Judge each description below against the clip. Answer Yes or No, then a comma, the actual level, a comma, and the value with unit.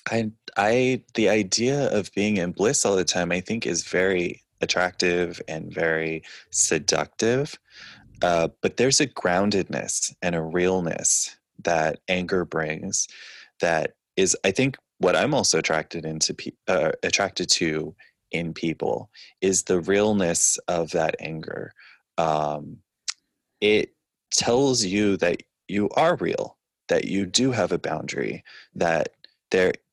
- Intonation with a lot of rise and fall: No, average, 3.8 semitones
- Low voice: Yes, very low, 90 Hz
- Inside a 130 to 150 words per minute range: Yes, slow, 135 wpm